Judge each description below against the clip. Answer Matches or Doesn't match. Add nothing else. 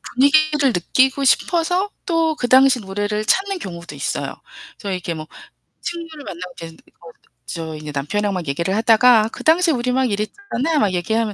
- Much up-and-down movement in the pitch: Matches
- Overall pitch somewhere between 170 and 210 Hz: Doesn't match